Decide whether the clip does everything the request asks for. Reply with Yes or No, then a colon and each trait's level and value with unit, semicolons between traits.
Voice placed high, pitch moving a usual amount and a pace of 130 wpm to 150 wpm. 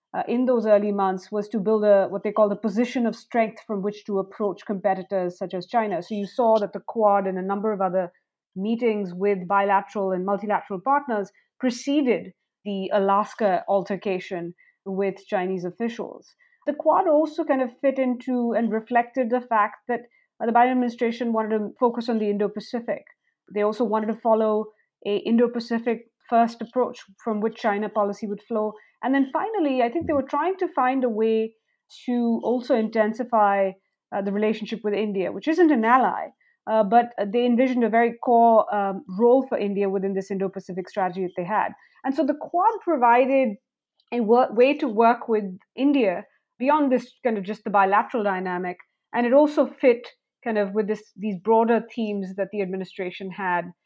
No: high, 220 Hz; average, 3.4 semitones; average, 185 wpm